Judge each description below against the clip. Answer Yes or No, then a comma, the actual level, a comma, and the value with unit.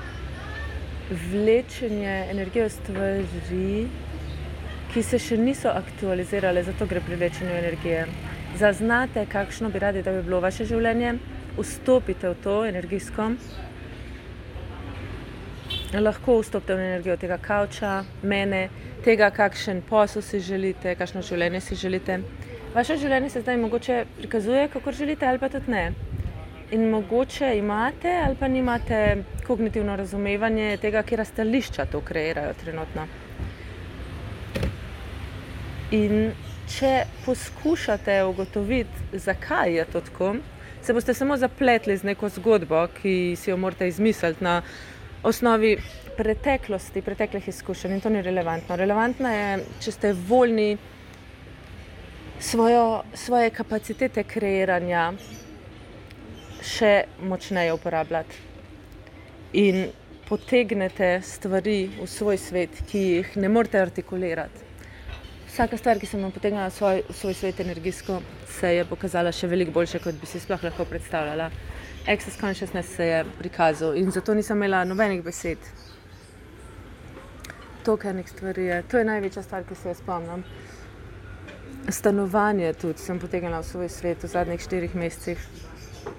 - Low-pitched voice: No, high, 190 Hz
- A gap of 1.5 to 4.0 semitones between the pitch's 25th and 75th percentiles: No, average, 4.7 semitones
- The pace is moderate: No, slow, 125 wpm